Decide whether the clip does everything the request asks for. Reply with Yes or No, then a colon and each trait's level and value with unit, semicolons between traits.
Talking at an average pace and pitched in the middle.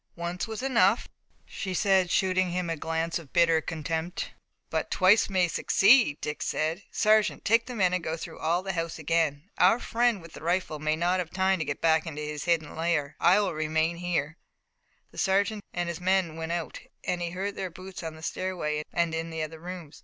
No: fast, 210 wpm; medium, 170 Hz